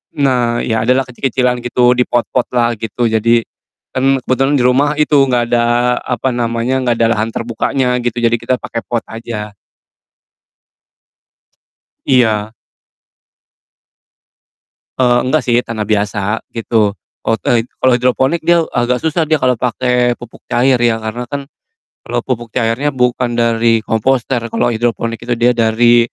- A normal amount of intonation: No, narrow, 1.7 semitones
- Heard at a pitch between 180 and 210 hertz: No, low, 120 Hz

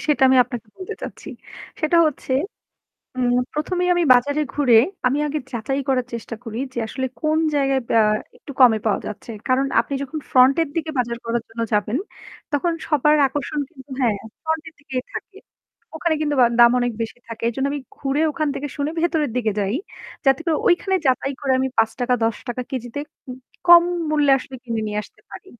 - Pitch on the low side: No, very high, 270 Hz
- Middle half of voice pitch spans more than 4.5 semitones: No, average, 4.1 semitones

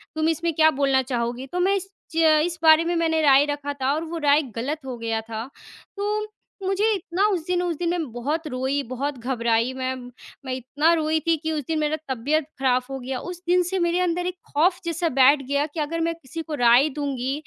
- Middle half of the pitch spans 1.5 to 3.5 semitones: No, average, 4.2 semitones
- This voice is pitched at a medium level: No, very high, 300 Hz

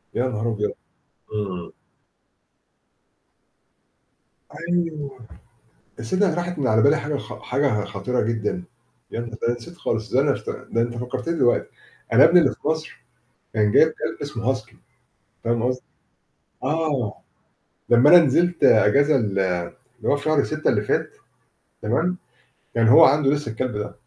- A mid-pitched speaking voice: No, low, 125 Hz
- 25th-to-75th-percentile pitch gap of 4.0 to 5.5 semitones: Yes, average, 5.2 semitones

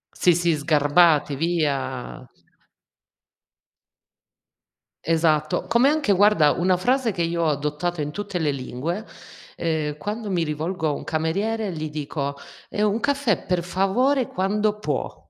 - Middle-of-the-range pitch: Yes, medium, 170 Hz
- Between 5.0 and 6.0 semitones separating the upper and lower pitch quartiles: Yes, wide, 5.4 semitones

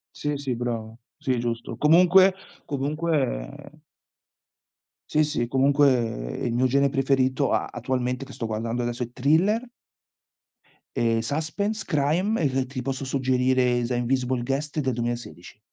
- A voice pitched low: Yes, low, 130 Hz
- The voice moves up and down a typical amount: Yes, average, 3.3 semitones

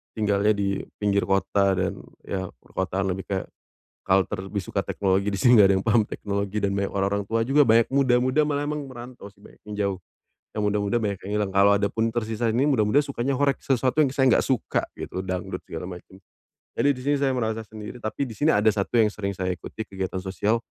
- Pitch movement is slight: No, average, 3.5 semitones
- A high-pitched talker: No, low, 105 Hz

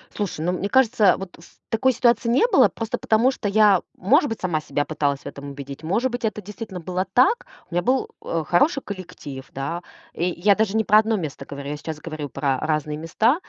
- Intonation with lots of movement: Yes, wide, 6.4 semitones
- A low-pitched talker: No, medium, 185 Hz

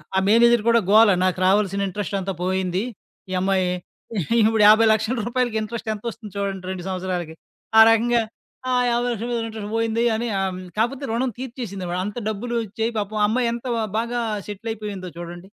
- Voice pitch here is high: Yes, high, 215 Hz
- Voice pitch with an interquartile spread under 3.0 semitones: No, average, 3.3 semitones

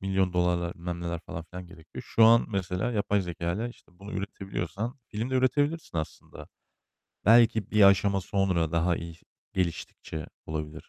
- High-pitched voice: No, very low, 95 Hz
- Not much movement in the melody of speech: No, average, 3.9 semitones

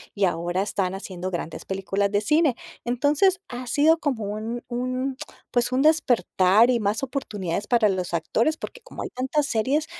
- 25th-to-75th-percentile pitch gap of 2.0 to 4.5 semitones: No, wide, 5.6 semitones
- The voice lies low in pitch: No, high, 235 Hz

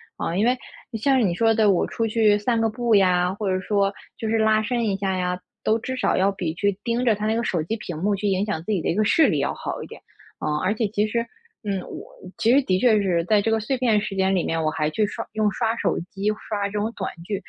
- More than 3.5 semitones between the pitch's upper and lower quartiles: No, average, 2.8 semitones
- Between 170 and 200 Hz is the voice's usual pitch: No, high, 210 Hz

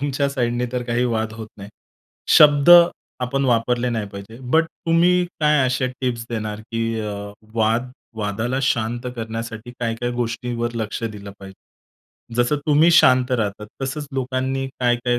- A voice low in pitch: Yes, low, 120 Hz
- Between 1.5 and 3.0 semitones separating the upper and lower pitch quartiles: Yes, narrow, 2.6 semitones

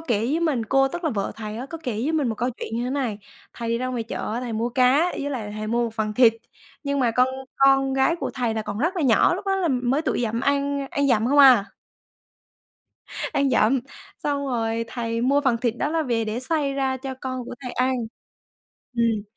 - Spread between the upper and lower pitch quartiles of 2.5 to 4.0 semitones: Yes, average, 3.3 semitones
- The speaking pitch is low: No, very high, 255 Hz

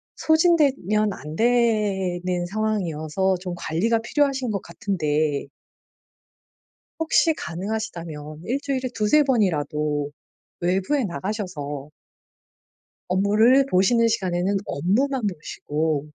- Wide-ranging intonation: Yes, wide, 5.9 semitones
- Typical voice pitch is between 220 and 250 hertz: No, high, 195 Hz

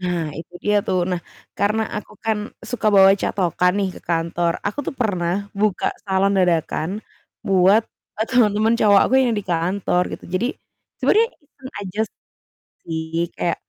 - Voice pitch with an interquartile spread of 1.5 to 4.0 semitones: Yes, average, 3.3 semitones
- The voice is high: Yes, high, 195 Hz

